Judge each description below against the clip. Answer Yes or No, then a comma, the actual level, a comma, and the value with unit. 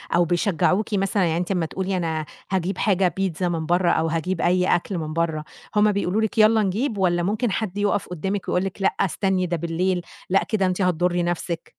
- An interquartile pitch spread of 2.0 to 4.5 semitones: Yes, narrow, 2.4 semitones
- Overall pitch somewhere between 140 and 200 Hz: Yes, medium, 185 Hz